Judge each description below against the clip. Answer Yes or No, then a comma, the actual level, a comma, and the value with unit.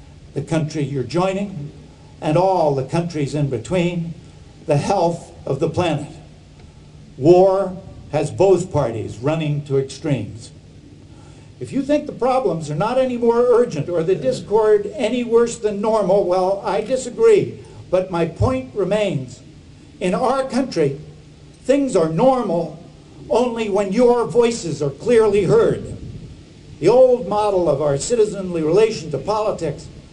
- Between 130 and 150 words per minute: Yes, slow, 135 wpm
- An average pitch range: No, wide, 6.9 semitones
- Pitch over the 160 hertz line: Yes, medium, 180 Hz